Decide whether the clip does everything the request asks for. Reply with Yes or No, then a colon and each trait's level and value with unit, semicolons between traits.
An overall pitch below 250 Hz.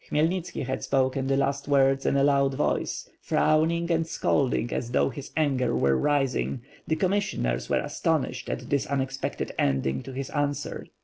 Yes: medium, 140 Hz